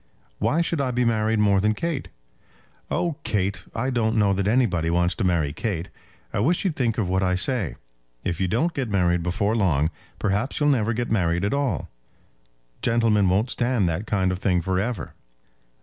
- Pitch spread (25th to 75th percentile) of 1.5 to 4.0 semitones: No, average, 4.7 semitones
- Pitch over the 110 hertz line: No, low, 105 Hz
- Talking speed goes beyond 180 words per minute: Yes, average, 190 wpm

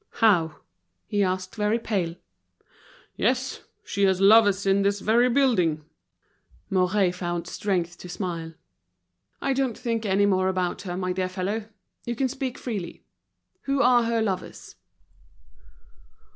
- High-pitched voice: Yes, high, 195 Hz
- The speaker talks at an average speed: No, slow, 130 wpm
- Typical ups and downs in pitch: Yes, average, 3.8 semitones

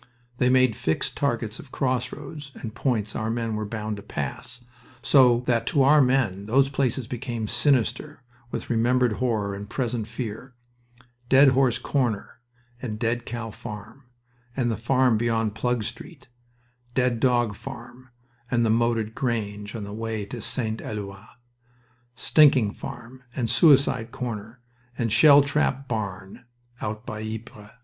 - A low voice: Yes, low, 120 Hz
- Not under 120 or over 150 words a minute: Yes, average, 145 wpm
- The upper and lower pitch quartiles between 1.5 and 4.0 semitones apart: Yes, average, 2.9 semitones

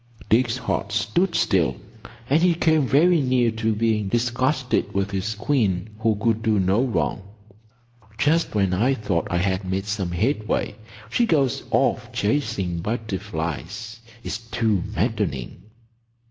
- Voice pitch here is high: No, low, 110 Hz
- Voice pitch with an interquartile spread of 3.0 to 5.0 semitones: Yes, average, 4.7 semitones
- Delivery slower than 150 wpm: Yes, slow, 135 wpm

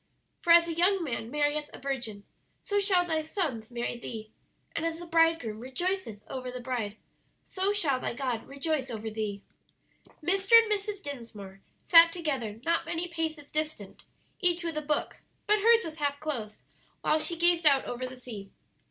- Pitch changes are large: Yes, wide, 6.0 semitones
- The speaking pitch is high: Yes, very high, 300 Hz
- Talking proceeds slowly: No, average, 175 wpm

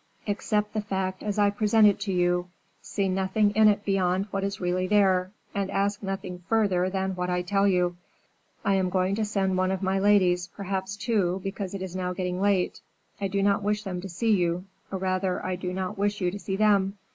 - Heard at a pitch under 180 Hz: No, high, 195 Hz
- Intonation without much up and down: Yes, narrow, 1.7 semitones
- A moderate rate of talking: No, fast, 215 wpm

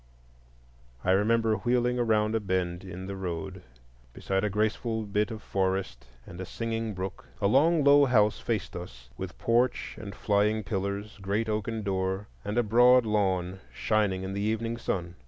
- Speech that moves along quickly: No, average, 165 wpm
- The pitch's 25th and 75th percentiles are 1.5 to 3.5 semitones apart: Yes, average, 3.0 semitones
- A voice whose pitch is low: Yes, low, 105 Hz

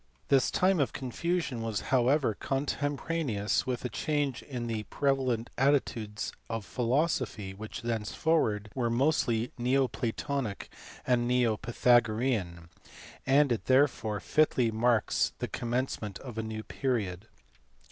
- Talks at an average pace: No, slow, 125 wpm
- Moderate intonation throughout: Yes, average, 3.6 semitones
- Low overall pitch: Yes, low, 120 Hz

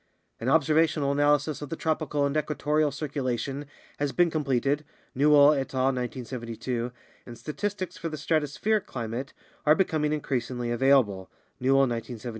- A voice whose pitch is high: No, medium, 140 Hz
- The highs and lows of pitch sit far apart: No, average, 3.2 semitones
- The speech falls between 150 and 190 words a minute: No, average, 140 wpm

